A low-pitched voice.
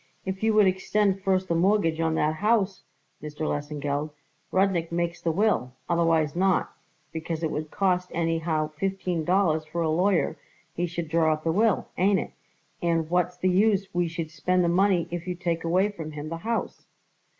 No: medium, 170 Hz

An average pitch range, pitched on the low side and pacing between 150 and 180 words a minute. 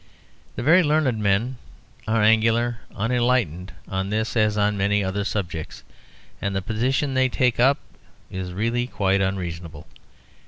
No: average, 4.0 semitones; low, 110 Hz; slow, 135 wpm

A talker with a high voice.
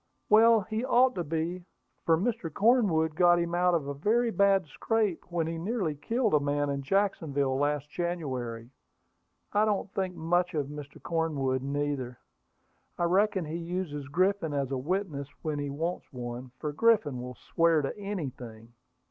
No: medium, 165 Hz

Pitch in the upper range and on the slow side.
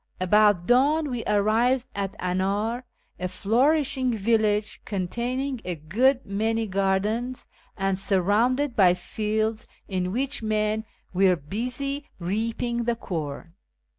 Yes: high, 215 Hz; slow, 115 wpm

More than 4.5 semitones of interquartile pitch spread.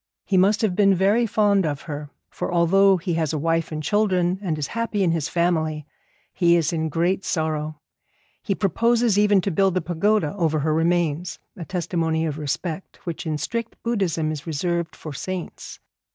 No: average, 3.6 semitones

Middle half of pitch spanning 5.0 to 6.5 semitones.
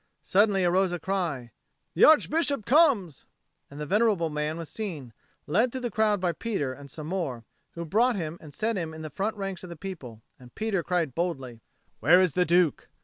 Yes: average, 5.3 semitones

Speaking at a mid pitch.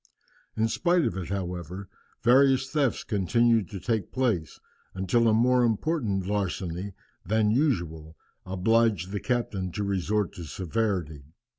No: low, 105 Hz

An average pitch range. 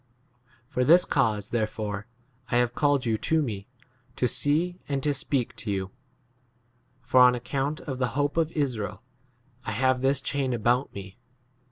Yes: average, 4.1 semitones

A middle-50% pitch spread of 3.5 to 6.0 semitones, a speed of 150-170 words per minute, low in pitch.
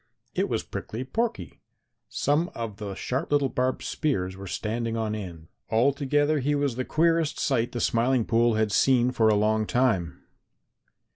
Yes: average, 4.5 semitones; average, 160 wpm; low, 120 Hz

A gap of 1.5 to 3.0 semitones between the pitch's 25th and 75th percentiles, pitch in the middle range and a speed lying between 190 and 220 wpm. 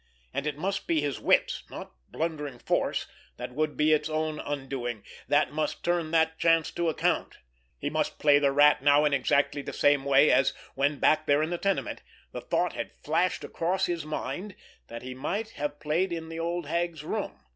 Yes: narrow, 2.6 semitones; medium, 150 Hz; average, 200 wpm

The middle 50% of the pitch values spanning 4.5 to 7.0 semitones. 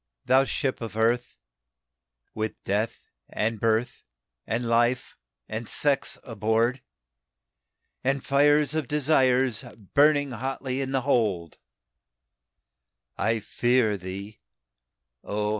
No: average, 3.5 semitones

